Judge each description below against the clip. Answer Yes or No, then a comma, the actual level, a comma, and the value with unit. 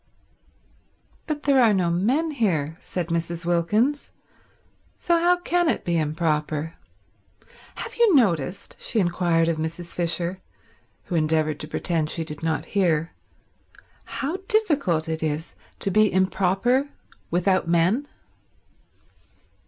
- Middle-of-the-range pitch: Yes, medium, 175 Hz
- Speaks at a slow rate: Yes, slow, 120 wpm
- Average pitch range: No, wide, 6.6 semitones